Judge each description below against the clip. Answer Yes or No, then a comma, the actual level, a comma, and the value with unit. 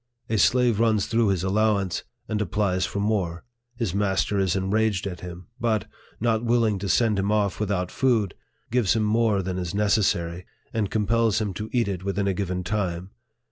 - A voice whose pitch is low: Yes, low, 100 Hz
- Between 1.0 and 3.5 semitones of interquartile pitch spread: Yes, average, 2.8 semitones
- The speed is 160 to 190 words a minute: Yes, average, 180 wpm